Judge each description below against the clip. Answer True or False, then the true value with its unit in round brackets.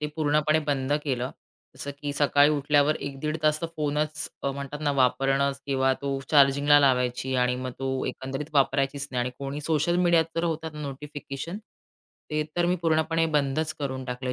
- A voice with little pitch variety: True (2.2 semitones)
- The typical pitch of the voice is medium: True (145 Hz)